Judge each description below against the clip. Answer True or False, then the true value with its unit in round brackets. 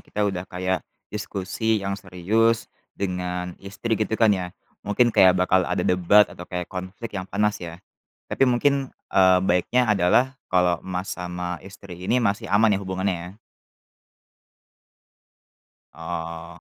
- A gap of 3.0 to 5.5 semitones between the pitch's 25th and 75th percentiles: False (2.6 semitones)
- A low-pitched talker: True (95 Hz)